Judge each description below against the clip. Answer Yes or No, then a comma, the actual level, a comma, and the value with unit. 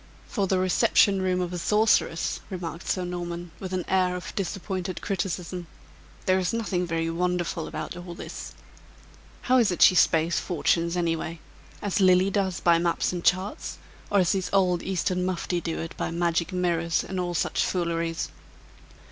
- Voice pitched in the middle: Yes, medium, 180 Hz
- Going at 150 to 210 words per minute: Yes, average, 170 wpm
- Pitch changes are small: Yes, narrow, 1.7 semitones